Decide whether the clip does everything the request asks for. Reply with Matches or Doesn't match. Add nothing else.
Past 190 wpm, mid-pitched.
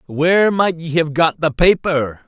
Doesn't match